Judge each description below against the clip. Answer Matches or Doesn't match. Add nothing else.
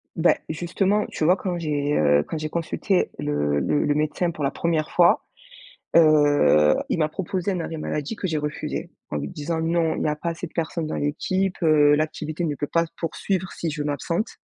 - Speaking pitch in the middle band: Matches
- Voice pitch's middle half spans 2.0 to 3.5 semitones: Matches